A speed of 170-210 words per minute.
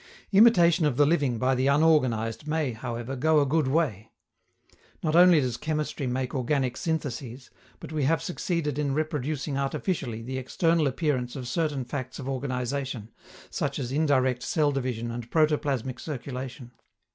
No: average, 150 wpm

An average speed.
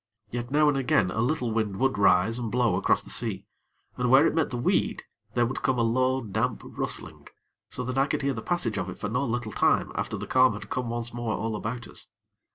No: fast, 240 wpm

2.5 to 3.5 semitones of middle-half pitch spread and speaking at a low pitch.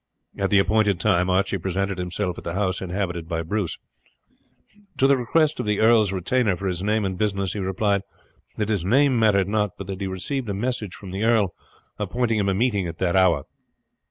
Yes: average, 2.8 semitones; low, 100 Hz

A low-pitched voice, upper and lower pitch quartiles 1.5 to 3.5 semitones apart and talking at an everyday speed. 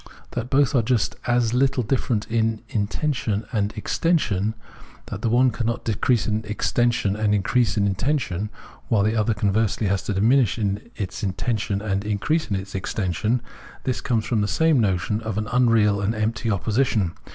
Yes: low, 110 Hz; average, 2.9 semitones; average, 165 wpm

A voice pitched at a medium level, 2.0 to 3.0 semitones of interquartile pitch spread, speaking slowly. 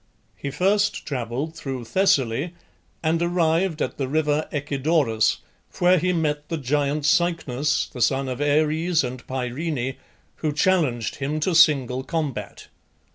No: medium, 150 Hz; average, 3.7 semitones; slow, 130 wpm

